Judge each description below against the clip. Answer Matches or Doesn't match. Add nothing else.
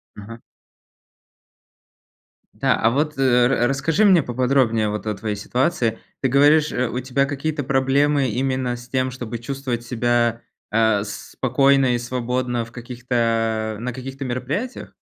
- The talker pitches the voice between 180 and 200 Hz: Doesn't match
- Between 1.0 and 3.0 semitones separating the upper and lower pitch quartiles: Matches